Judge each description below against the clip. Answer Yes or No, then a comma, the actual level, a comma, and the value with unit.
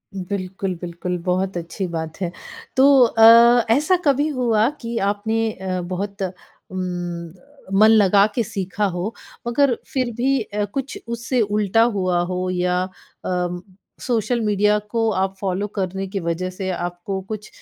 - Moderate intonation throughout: Yes, average, 3.8 semitones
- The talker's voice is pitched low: No, high, 195 Hz